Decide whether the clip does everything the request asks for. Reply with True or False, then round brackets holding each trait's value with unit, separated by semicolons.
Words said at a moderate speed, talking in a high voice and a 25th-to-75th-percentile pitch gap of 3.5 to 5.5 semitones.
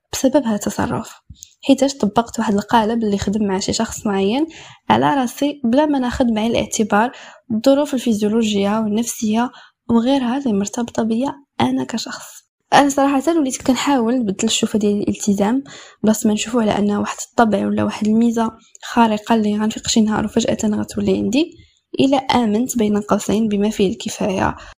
False (150 wpm; 230 Hz; 3.8 semitones)